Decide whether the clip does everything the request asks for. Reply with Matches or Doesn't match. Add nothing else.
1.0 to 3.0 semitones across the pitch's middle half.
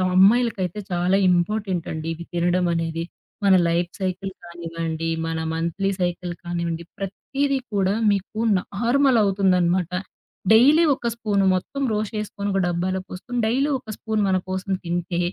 Doesn't match